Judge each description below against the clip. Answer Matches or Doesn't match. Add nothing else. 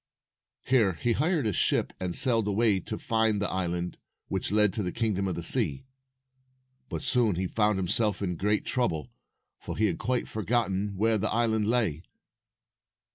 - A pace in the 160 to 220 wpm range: Matches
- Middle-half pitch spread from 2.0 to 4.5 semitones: Matches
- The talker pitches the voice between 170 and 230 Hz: Doesn't match